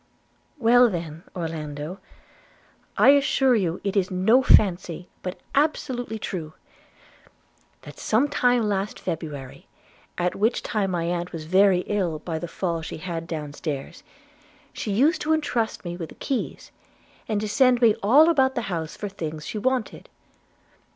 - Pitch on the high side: Yes, high, 195 Hz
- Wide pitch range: Yes, wide, 6.4 semitones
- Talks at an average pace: Yes, average, 150 wpm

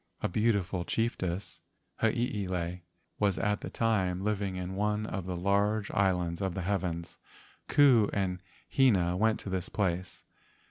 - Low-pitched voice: Yes, very low, 95 Hz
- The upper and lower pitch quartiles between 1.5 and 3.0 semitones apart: Yes, average, 2.7 semitones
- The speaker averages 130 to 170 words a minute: Yes, average, 140 wpm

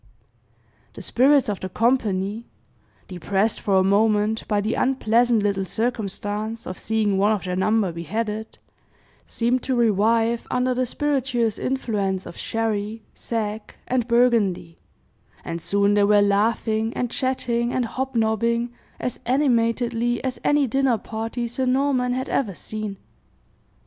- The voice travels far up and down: No, average, 3.0 semitones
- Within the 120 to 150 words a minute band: Yes, slow, 135 wpm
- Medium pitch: No, high, 225 Hz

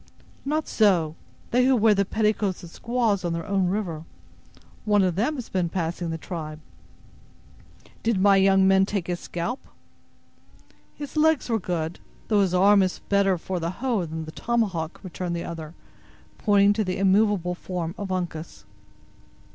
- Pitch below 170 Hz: No, high, 190 Hz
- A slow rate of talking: No, average, 165 wpm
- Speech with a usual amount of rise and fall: Yes, average, 3.6 semitones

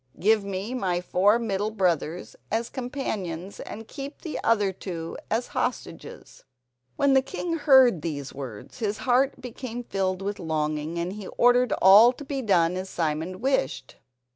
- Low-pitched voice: No, high, 200 Hz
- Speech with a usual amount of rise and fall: No, wide, 5.8 semitones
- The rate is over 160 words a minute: No, average, 155 wpm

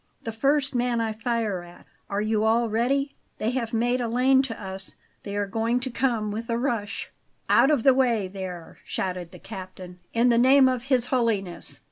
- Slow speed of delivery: No, average, 195 wpm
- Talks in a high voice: Yes, high, 230 Hz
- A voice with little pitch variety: No, average, 3.6 semitones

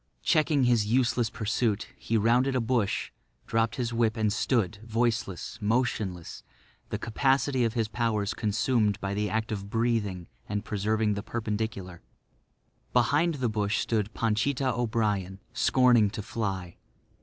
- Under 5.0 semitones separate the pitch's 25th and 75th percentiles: Yes, average, 2.7 semitones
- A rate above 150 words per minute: No, slow, 135 wpm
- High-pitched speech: No, low, 110 Hz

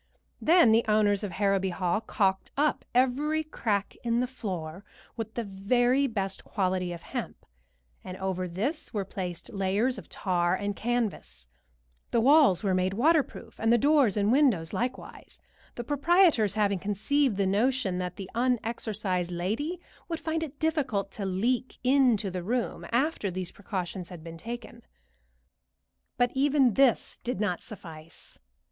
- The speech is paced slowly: No, average, 150 wpm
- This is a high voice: Yes, high, 215 Hz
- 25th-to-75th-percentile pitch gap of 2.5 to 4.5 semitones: No, average, 5.3 semitones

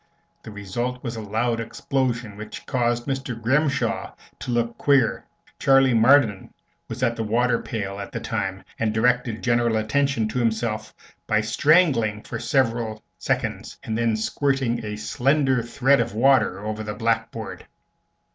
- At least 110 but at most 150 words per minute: Yes, average, 145 wpm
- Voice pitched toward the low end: Yes, low, 115 Hz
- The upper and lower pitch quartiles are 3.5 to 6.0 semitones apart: No, average, 2.8 semitones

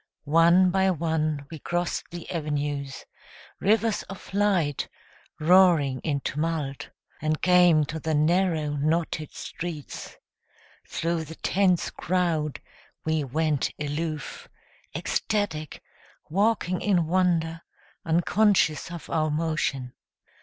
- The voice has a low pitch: No, medium, 160 Hz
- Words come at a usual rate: No, slow, 105 wpm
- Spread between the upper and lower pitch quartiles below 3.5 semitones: Yes, average, 3.0 semitones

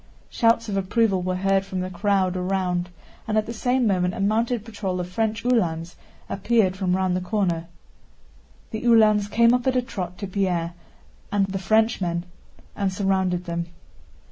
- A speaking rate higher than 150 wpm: Yes, average, 170 wpm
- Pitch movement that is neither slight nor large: Yes, average, 3.3 semitones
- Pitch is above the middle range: Yes, high, 195 Hz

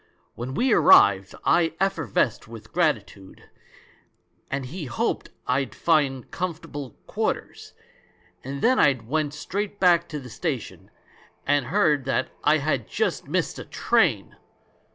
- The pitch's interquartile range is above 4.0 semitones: Yes, average, 5.0 semitones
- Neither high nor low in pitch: Yes, medium, 145 Hz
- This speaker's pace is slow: Yes, slow, 130 wpm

